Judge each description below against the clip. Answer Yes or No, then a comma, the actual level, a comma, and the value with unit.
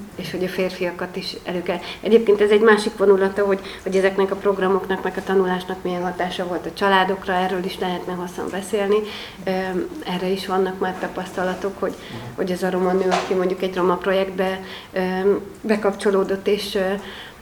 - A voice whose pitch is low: No, high, 190 Hz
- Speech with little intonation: Yes, narrow, 1.2 semitones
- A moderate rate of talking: No, fast, 165 wpm